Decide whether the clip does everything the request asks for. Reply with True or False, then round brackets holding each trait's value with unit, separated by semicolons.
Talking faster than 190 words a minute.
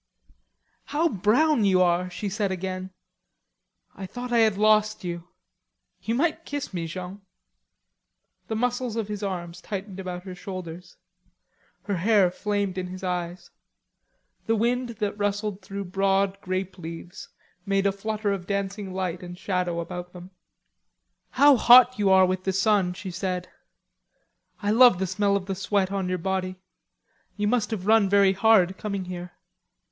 False (155 wpm)